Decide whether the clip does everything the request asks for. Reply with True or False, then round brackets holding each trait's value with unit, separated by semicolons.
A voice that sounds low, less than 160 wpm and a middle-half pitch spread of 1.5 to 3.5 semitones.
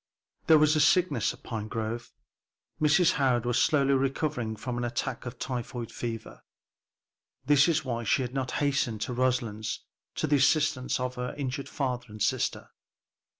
True (125 Hz; 150 wpm; 3.1 semitones)